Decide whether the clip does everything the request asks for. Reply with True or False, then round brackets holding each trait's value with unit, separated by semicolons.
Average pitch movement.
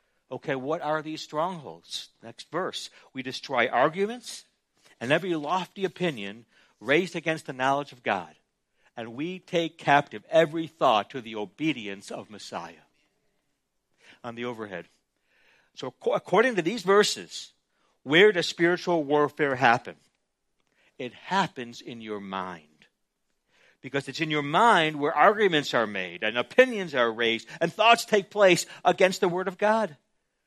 False (6.8 semitones)